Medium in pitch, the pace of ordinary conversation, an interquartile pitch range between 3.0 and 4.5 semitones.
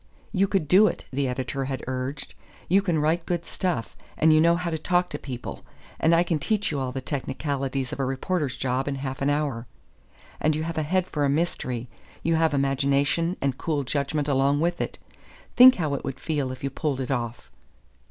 No: medium, 145 Hz; fast, 210 wpm; average, 3.7 semitones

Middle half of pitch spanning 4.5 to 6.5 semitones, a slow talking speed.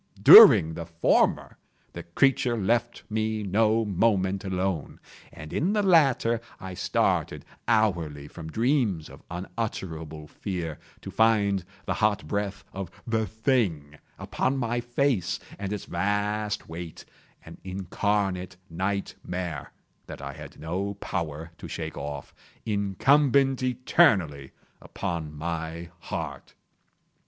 Yes: average, 5.0 semitones; slow, 110 wpm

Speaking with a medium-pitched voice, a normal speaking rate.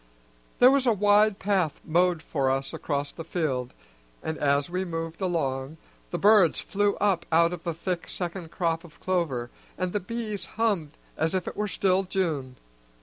Yes: medium, 175 Hz; average, 175 wpm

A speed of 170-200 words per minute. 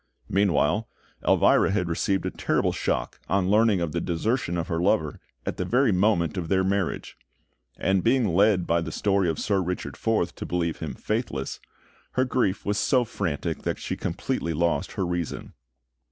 Yes: average, 175 wpm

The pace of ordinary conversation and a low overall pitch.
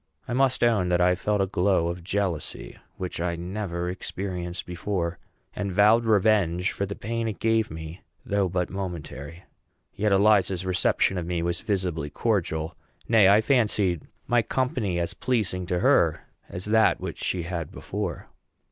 Yes: average, 160 wpm; very low, 95 Hz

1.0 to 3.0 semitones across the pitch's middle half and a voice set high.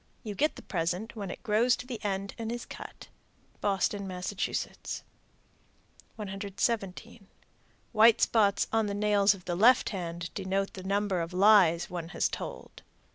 Yes: narrow, 2.6 semitones; high, 200 Hz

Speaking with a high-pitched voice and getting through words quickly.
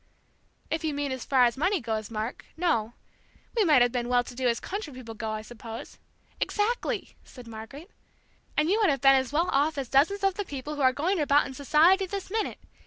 Yes: very high, 280 Hz; fast, 225 wpm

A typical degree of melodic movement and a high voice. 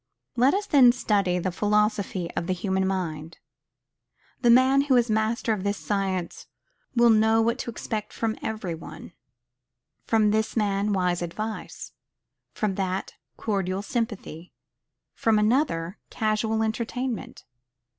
Yes: average, 3.1 semitones; high, 215 Hz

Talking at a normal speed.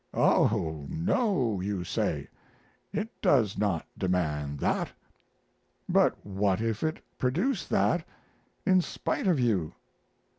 No: slow, 110 wpm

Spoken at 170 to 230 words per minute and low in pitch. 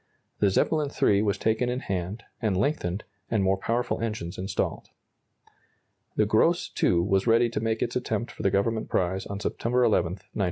Yes: average, 175 wpm; low, 105 Hz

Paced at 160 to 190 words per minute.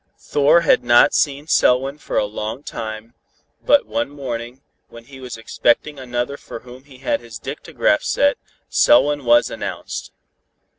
No: average, 150 wpm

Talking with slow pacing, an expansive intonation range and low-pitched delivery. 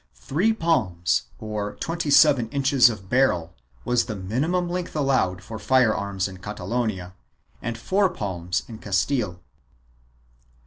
Yes: slow, 130 wpm; wide, 6.7 semitones; low, 110 Hz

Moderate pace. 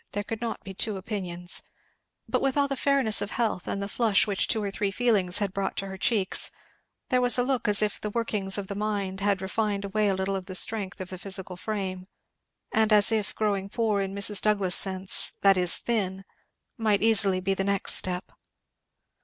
No: fast, 210 wpm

